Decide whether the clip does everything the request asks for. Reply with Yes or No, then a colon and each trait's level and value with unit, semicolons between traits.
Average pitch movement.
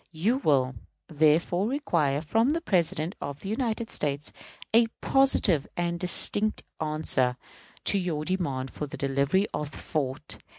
No: wide, 6.3 semitones